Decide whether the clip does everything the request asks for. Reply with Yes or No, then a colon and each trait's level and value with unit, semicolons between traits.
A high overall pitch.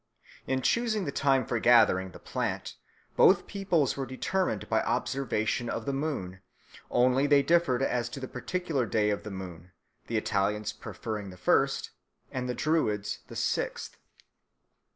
No: low, 125 Hz